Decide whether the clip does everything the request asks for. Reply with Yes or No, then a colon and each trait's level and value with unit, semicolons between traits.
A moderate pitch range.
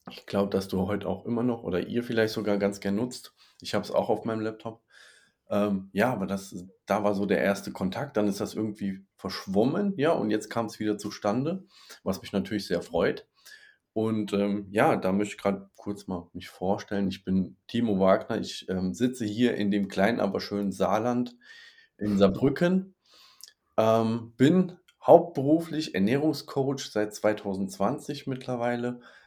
Yes: average, 3.6 semitones